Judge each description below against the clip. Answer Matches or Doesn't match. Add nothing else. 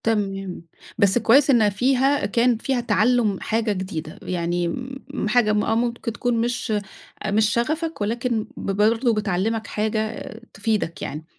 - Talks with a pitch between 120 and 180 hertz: Doesn't match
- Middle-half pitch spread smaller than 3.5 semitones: Matches